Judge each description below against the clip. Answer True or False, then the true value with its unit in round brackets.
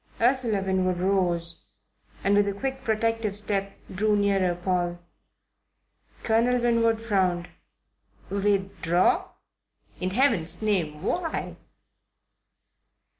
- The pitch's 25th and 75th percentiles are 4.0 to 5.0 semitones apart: False (3.6 semitones)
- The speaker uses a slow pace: True (90 wpm)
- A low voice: False (200 Hz)